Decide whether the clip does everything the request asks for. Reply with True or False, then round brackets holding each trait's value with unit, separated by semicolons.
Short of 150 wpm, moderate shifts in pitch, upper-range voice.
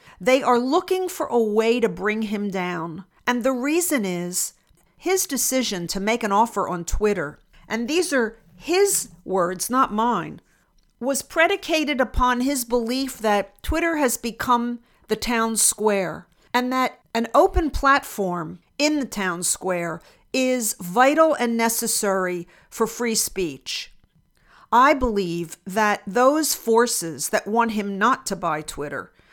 True (140 wpm; 5.0 semitones; 230 Hz)